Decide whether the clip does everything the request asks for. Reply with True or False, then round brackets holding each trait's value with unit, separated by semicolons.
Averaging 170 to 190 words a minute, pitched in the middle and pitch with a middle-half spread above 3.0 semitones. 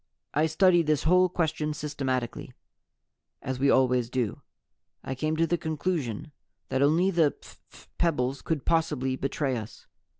False (140 wpm; 150 Hz; 3.8 semitones)